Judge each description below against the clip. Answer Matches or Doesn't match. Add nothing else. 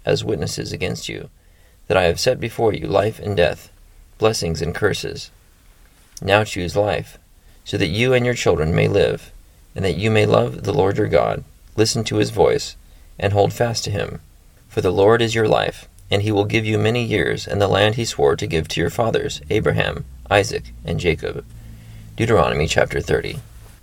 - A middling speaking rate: Matches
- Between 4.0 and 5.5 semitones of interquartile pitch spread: Matches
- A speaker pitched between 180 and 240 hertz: Doesn't match